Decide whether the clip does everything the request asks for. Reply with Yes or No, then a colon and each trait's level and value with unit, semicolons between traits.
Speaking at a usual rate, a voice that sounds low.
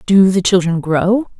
No: average, 170 wpm; high, 190 Hz